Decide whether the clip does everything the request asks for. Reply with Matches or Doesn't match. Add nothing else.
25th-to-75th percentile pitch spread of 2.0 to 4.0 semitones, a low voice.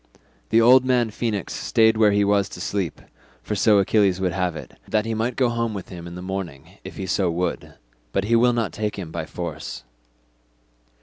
Matches